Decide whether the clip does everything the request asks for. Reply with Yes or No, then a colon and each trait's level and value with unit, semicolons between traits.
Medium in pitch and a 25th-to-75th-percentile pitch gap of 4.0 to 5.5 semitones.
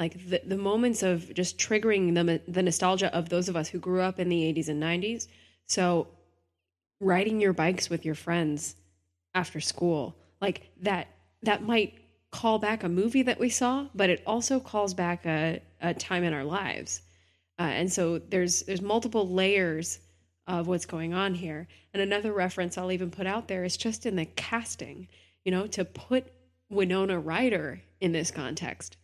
No: medium, 180 Hz; average, 3.6 semitones